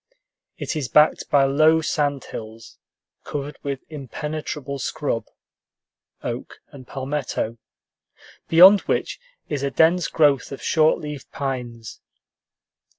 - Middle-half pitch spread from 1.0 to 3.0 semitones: Yes, narrow, 2.6 semitones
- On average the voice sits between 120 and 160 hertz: Yes, medium, 140 Hz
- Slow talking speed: Yes, slow, 110 wpm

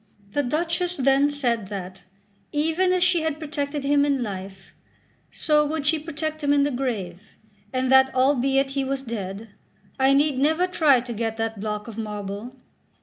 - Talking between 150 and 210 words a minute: Yes, average, 170 wpm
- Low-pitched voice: No, very high, 270 Hz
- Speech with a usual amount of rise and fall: Yes, average, 4.9 semitones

